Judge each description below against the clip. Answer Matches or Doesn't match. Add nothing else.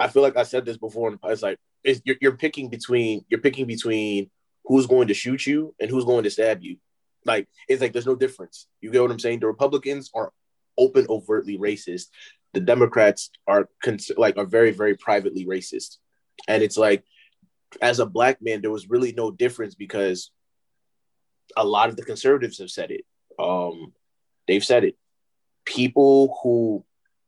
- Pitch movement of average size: Matches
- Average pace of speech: Matches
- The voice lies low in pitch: Matches